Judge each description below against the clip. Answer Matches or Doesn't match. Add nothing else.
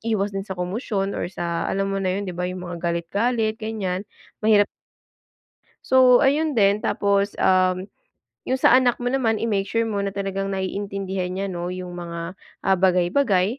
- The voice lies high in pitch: Matches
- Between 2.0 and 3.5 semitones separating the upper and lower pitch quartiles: Matches